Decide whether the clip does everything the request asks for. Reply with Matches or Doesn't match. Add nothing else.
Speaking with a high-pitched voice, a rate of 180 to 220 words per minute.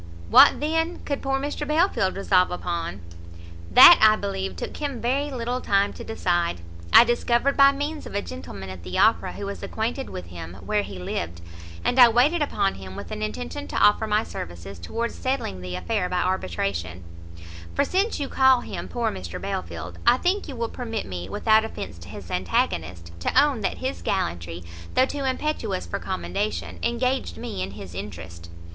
Matches